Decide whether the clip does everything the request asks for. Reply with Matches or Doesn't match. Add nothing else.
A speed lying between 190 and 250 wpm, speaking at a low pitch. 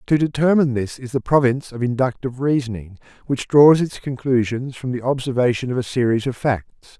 Doesn't match